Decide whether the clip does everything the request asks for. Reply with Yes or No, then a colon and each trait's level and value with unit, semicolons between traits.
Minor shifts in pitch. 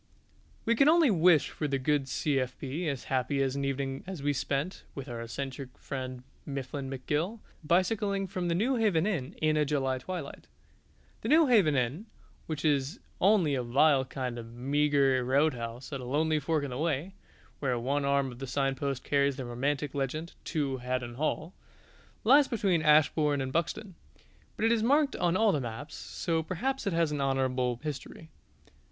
No: average, 4.3 semitones